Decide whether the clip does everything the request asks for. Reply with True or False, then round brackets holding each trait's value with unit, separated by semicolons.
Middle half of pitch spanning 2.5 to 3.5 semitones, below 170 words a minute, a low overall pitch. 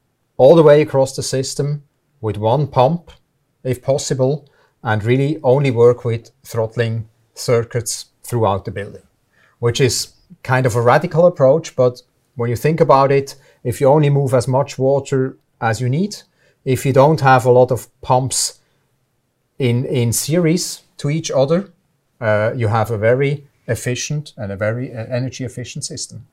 True (3.2 semitones; 160 wpm; 130 Hz)